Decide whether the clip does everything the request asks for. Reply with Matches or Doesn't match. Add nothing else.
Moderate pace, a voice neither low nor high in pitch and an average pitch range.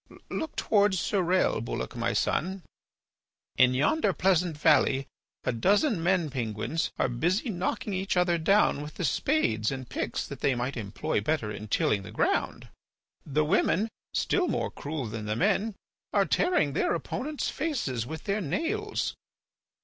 Doesn't match